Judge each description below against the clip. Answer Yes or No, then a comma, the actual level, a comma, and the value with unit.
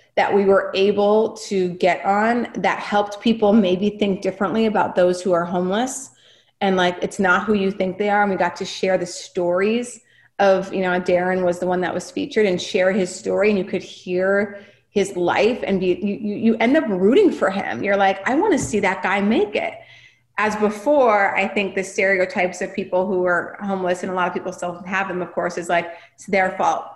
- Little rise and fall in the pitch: Yes, narrow, 2.2 semitones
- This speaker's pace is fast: Yes, fast, 220 wpm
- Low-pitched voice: No, high, 195 Hz